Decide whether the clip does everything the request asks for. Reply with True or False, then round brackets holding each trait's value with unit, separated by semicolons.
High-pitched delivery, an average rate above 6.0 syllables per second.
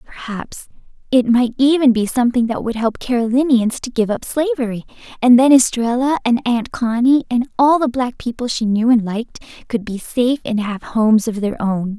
False (240 Hz; 5.2 syllables/s)